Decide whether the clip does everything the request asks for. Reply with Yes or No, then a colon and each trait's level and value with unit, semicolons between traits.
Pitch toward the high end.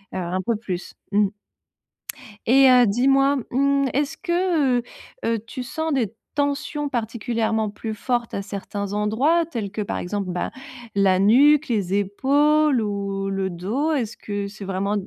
Yes: high, 225 Hz